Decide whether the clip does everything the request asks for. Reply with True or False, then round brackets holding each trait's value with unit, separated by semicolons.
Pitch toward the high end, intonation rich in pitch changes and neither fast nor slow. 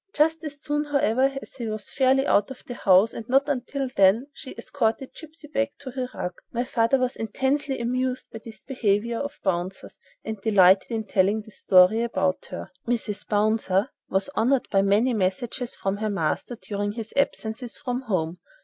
False (230 Hz; 4.5 semitones; 180 wpm)